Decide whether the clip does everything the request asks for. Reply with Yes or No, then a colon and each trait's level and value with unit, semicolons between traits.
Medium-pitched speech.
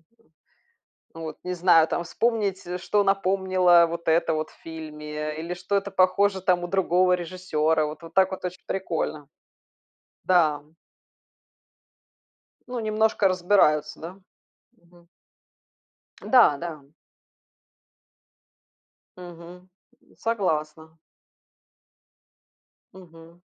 Yes: medium, 175 Hz